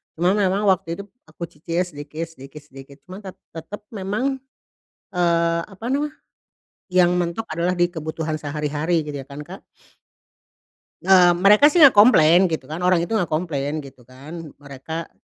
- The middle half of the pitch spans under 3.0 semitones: No, average, 3.6 semitones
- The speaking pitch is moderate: Yes, medium, 170 Hz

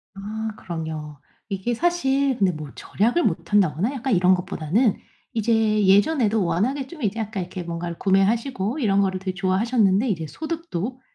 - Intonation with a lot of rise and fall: No, average, 4.5 semitones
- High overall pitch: Yes, high, 205 Hz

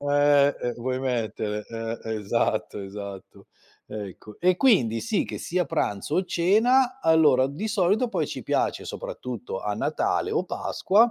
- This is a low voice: No, medium, 145 Hz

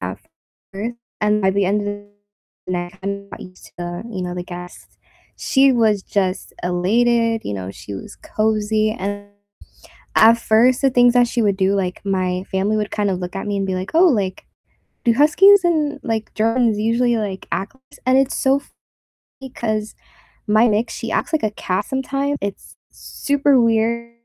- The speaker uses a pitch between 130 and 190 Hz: No, high, 215 Hz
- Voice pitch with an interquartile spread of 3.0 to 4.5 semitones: Yes, average, 3.9 semitones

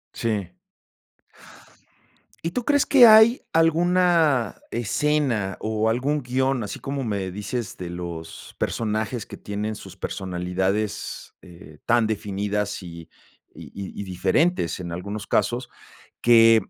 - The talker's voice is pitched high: No, low, 110 Hz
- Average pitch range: No, wide, 5.8 semitones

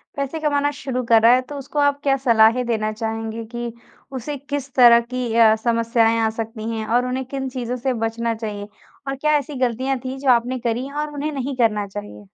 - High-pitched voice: Yes, high, 245 Hz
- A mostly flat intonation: No, average, 3.2 semitones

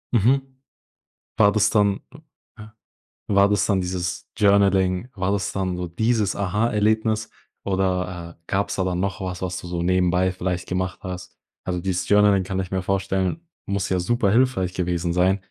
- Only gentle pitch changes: Yes, narrow, 2.2 semitones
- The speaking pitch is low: Yes, very low, 95 Hz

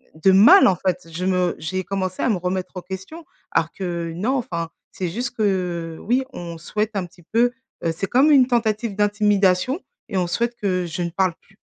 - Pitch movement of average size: Yes, average, 3.6 semitones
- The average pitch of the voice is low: No, high, 190 Hz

